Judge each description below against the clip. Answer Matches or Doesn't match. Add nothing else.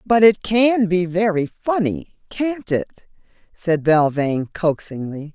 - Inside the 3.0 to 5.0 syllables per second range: Matches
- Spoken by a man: Doesn't match